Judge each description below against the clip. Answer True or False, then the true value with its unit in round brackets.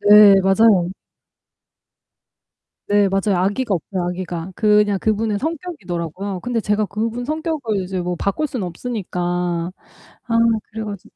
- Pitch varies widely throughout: False (3.6 semitones)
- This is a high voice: True (205 Hz)